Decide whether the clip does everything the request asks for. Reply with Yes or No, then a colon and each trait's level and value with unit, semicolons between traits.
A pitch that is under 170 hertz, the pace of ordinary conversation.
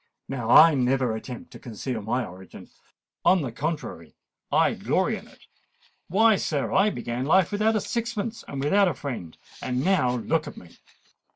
Yes: medium, 140 Hz; average, 170 wpm